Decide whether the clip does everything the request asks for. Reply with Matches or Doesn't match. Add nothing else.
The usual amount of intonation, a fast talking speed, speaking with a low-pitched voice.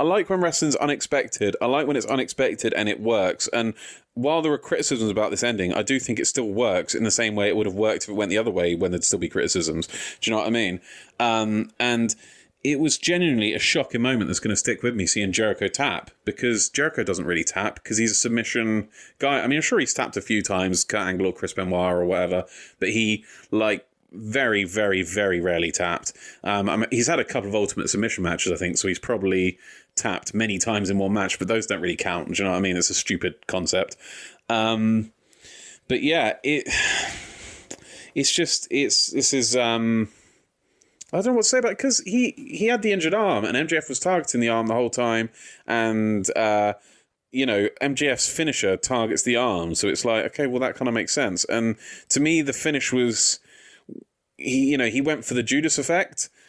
Matches